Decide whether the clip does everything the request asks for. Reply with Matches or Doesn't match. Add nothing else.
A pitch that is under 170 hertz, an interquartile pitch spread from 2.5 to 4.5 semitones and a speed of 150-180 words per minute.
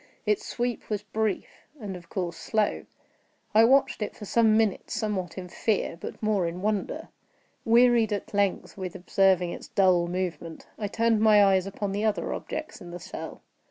Doesn't match